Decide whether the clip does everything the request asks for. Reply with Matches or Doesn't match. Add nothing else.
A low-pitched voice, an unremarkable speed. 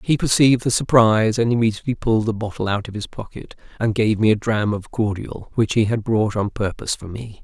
Doesn't match